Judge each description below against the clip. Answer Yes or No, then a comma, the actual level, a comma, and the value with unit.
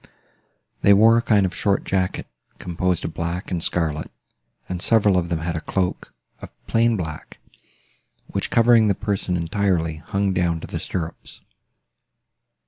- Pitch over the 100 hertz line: No, very low, 90 Hz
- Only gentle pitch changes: No, average, 3.3 semitones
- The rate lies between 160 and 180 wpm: No, average, 150 wpm